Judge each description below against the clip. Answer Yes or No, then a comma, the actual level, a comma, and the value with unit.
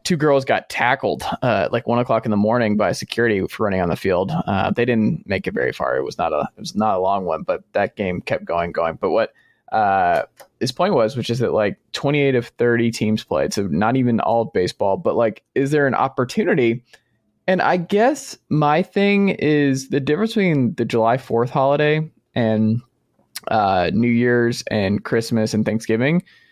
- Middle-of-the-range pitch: No, low, 120 Hz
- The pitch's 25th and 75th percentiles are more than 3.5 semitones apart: Yes, average, 4.6 semitones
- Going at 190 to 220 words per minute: Yes, fast, 205 wpm